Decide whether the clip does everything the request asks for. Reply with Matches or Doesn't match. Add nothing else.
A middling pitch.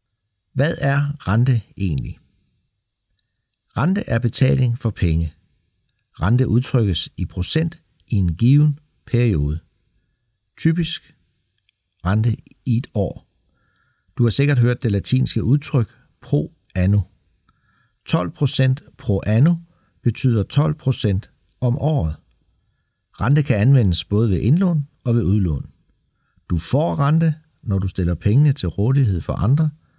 Doesn't match